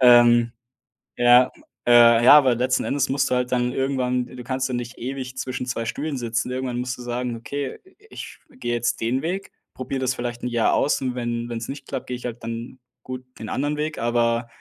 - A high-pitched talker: No, low, 125 Hz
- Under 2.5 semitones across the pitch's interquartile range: Yes, narrow, 1.7 semitones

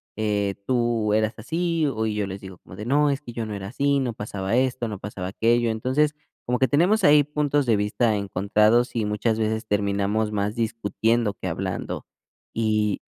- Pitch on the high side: No, low, 110 Hz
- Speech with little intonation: No, average, 3.5 semitones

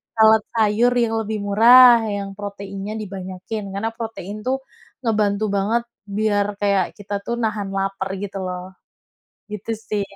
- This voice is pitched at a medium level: No, high, 205 Hz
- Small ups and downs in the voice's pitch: Yes, narrow, 1.9 semitones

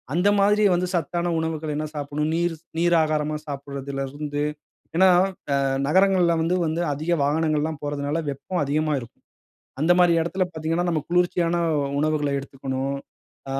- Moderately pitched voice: Yes, medium, 155 Hz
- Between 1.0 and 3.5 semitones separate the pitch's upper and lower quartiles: Yes, average, 3.0 semitones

